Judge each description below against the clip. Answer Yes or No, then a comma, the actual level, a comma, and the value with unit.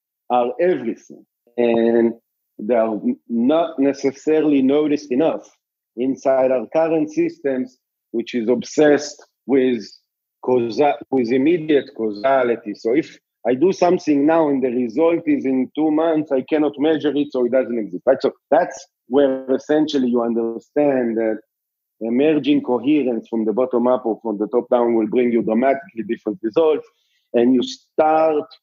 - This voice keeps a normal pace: Yes, average, 150 wpm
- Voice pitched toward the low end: Yes, low, 130 Hz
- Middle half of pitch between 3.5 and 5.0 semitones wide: Yes, average, 4.2 semitones